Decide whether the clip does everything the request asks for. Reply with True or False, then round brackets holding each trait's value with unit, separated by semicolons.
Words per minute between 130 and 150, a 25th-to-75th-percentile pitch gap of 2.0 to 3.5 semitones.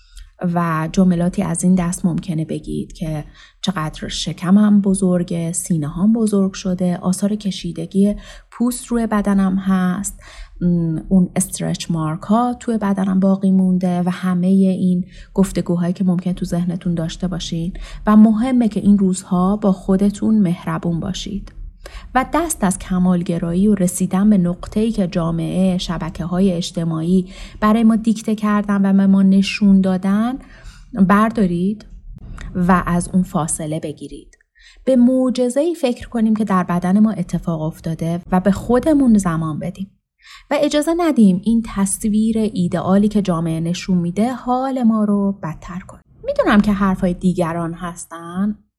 True (140 wpm; 3.1 semitones)